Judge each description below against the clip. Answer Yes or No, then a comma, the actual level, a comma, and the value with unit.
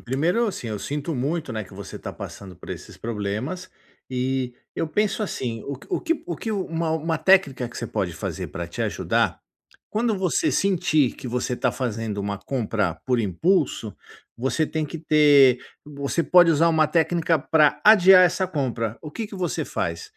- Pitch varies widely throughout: Yes, wide, 6.2 semitones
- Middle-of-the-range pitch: Yes, medium, 150 Hz